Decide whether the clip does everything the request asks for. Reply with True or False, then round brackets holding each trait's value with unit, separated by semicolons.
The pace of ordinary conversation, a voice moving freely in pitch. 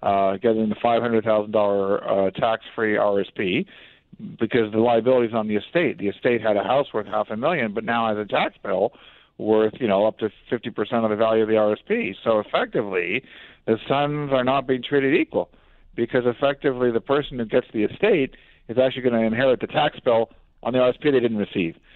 False (195 wpm; 2.8 semitones)